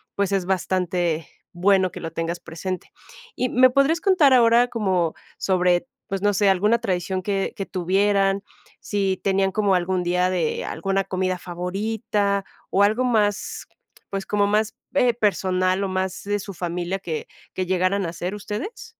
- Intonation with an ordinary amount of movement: No, narrow, 2.2 semitones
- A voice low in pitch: No, high, 195 Hz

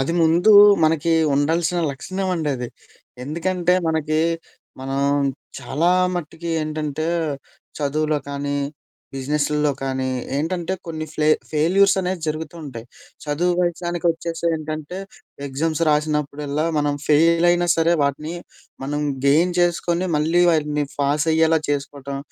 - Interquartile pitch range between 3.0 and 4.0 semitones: No, narrow, 2.6 semitones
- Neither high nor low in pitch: Yes, medium, 155 Hz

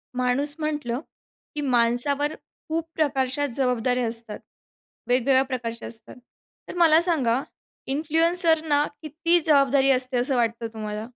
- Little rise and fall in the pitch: No, average, 4.0 semitones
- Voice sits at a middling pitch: No, very high, 270 Hz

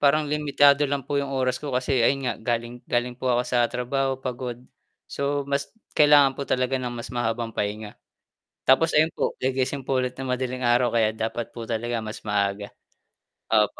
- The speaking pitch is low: Yes, low, 125 Hz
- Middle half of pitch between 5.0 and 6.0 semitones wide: No, average, 2.7 semitones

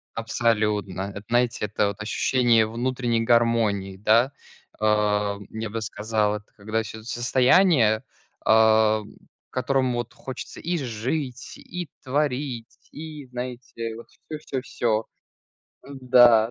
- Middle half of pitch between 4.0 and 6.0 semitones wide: No, average, 2.9 semitones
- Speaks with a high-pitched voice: No, low, 115 Hz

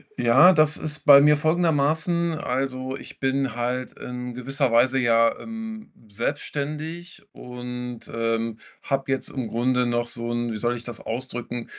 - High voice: No, low, 130 Hz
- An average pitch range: Yes, average, 3.8 semitones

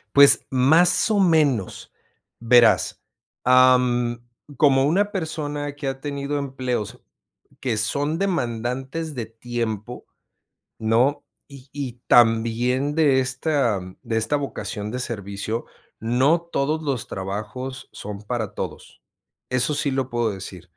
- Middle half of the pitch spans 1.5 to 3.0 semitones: No, average, 4.0 semitones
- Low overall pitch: Yes, low, 130 Hz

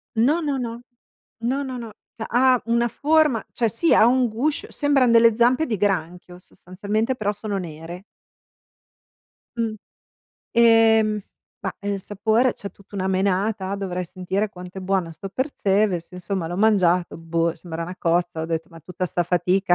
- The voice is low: No, high, 200 Hz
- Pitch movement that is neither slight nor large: Yes, average, 4.5 semitones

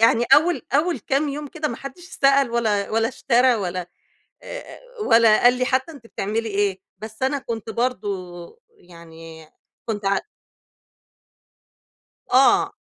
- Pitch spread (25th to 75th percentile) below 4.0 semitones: No, average, 5.0 semitones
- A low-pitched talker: No, high, 235 Hz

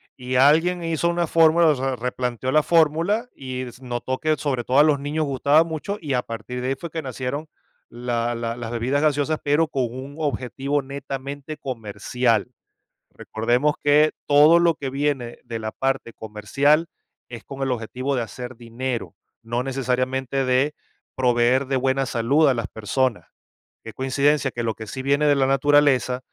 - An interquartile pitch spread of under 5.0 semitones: Yes, average, 3.1 semitones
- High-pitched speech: No, low, 135 Hz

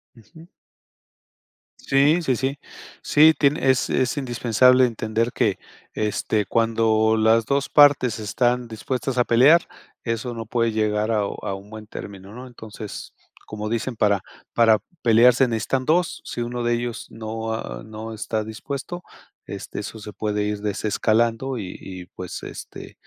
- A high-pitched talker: No, low, 115 Hz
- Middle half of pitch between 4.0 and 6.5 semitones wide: No, average, 2.9 semitones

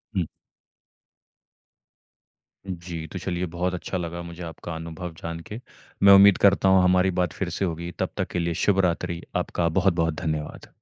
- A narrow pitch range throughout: Yes, narrow, 1.7 semitones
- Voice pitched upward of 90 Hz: No, very low, 85 Hz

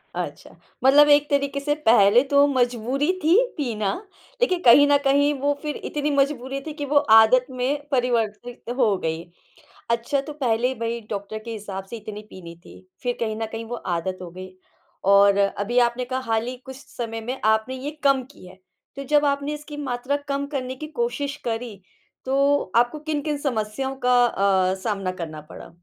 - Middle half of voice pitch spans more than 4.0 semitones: Yes, average, 4.5 semitones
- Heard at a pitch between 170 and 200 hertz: No, very high, 250 Hz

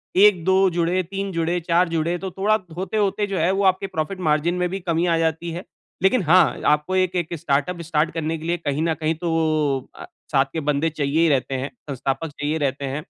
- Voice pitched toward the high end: No, medium, 170 Hz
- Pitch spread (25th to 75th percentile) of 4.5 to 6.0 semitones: No, average, 3.2 semitones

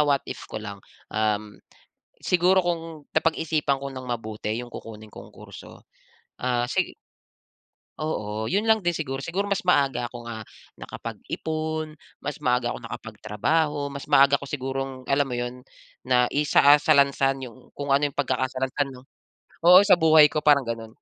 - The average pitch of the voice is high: No, medium, 140 Hz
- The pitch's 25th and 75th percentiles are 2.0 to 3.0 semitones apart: No, average, 4.2 semitones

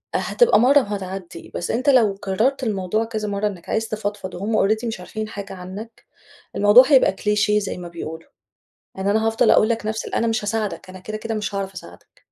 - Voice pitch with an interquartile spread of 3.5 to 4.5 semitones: No, average, 2.7 semitones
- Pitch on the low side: No, high, 210 Hz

